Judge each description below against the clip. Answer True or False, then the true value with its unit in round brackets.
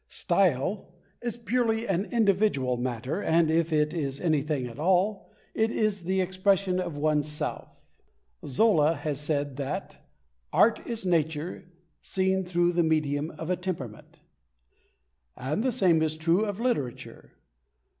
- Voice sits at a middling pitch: True (170 Hz)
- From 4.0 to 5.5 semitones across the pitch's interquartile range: True (4.6 semitones)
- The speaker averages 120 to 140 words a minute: True (135 wpm)